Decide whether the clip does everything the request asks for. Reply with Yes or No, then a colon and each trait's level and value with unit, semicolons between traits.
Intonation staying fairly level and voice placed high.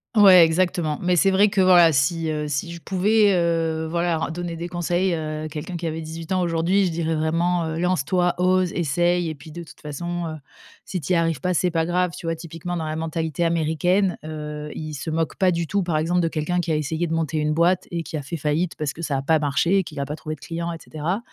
No: narrow, 2.1 semitones; medium, 165 Hz